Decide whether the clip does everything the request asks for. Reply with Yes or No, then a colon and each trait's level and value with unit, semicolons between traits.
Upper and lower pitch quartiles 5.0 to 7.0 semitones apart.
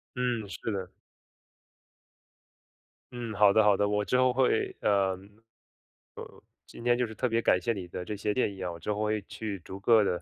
No: average, 3.1 semitones